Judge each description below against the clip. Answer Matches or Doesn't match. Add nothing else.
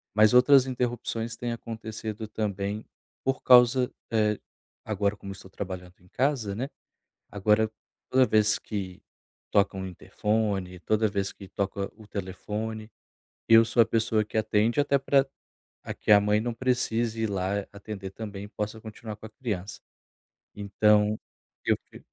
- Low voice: Matches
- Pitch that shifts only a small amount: Matches